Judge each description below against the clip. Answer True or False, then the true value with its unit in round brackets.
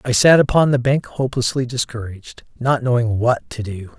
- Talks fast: False (180 wpm)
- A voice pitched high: False (120 Hz)